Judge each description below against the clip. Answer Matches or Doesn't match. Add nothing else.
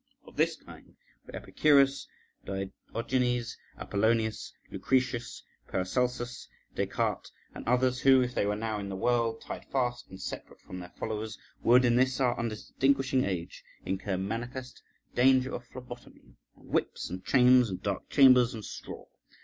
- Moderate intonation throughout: Matches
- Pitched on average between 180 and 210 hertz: Doesn't match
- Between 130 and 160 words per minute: Matches